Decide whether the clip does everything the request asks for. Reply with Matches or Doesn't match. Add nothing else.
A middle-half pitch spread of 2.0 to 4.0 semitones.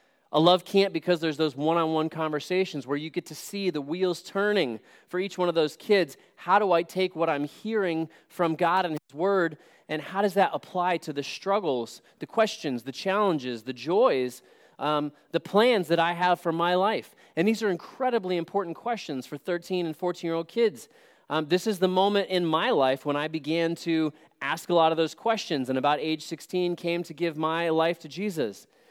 Matches